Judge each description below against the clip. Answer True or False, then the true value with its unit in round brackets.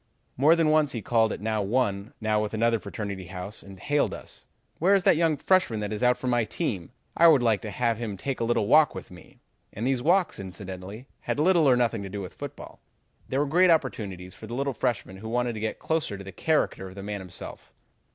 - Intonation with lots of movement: True (6.1 semitones)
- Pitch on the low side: True (115 Hz)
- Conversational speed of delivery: False (230 wpm)